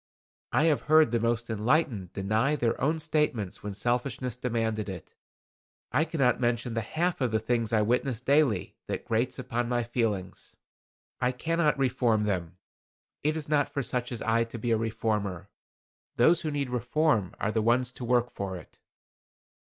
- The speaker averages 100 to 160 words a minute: No, average, 170 wpm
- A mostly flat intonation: No, average, 3.8 semitones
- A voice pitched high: No, low, 120 Hz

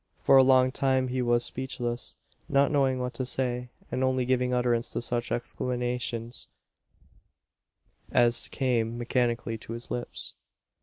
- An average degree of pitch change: No, narrow, 1.4 semitones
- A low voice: Yes, low, 125 Hz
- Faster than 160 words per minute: No, average, 140 wpm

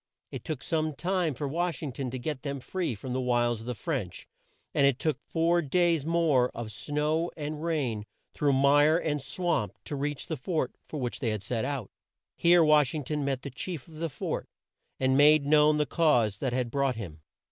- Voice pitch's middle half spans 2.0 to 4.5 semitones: Yes, average, 3.8 semitones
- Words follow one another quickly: Yes, fast, 210 wpm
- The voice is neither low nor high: Yes, medium, 145 Hz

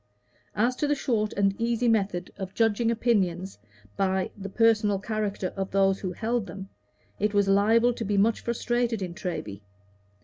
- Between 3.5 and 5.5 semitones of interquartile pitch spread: No, average, 3.0 semitones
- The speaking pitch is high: Yes, high, 205 Hz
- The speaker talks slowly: No, average, 165 wpm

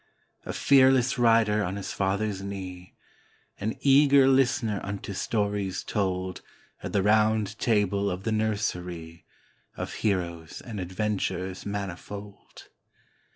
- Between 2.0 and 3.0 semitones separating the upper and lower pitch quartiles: Yes, average, 2.7 semitones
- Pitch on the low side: Yes, low, 100 Hz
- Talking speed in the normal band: No, slow, 110 wpm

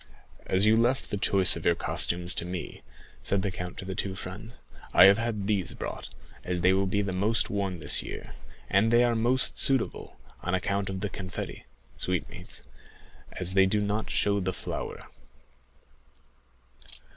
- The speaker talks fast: No, average, 175 wpm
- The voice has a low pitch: Yes, low, 100 Hz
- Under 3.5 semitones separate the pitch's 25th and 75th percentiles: Yes, narrow, 2.4 semitones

